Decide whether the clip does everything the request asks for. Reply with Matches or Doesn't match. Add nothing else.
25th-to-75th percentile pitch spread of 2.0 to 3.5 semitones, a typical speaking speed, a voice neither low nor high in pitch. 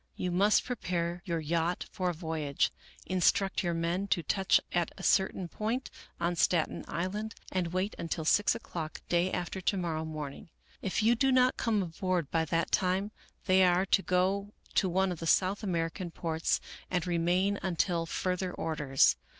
Matches